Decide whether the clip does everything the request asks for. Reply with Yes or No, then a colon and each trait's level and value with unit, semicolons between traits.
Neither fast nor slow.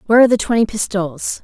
No: fast, 210 wpm